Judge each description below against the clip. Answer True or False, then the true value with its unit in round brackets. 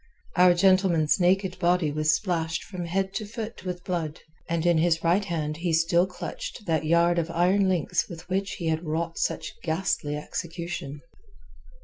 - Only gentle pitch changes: True (2.3 semitones)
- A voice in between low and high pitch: True (175 Hz)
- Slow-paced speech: False (165 wpm)